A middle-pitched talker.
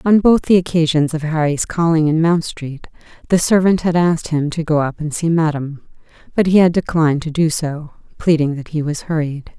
Yes: medium, 160 Hz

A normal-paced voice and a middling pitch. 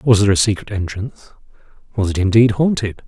No: average, 175 wpm; low, 105 Hz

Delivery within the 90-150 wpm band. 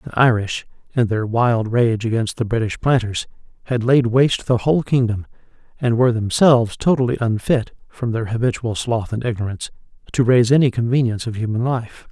No: average, 170 wpm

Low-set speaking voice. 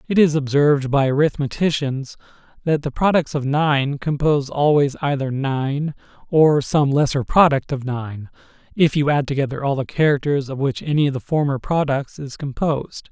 No: medium, 145 Hz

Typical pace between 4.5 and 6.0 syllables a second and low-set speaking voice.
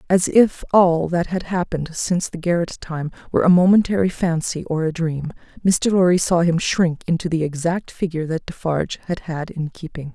No: 5.4 syllables/s; medium, 170 Hz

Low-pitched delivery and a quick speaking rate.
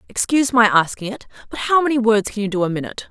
No: high, 220 Hz; fast, 250 wpm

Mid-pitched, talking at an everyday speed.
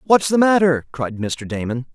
Yes: medium, 150 Hz; average, 185 wpm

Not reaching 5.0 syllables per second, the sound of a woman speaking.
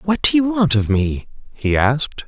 No: 4.7 syllables/s; male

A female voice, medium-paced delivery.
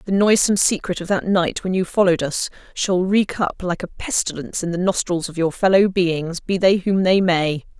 No: female; fast, 215 wpm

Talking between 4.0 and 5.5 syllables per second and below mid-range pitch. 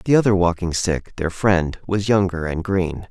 Yes: 4.6 syllables/s; very low, 90 Hz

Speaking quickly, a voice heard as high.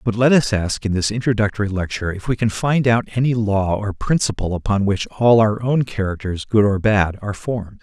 No: fast, 215 wpm; low, 105 Hz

